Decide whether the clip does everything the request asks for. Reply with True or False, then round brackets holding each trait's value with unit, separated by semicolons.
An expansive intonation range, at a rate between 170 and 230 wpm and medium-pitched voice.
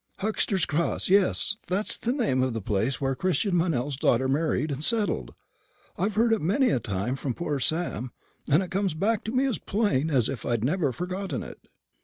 True (7.4 semitones; 195 wpm; 165 Hz)